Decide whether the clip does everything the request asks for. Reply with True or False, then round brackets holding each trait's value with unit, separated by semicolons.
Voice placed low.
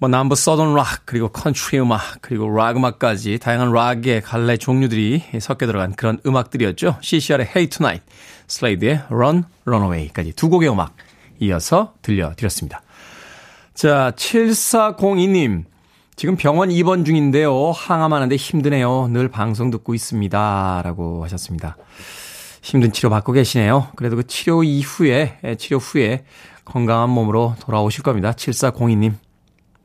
True (125 Hz)